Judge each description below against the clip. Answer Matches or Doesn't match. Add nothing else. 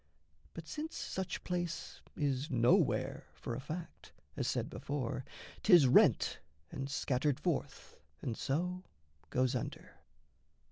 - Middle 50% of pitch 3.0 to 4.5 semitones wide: Doesn't match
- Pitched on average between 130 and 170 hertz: Matches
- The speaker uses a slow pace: Matches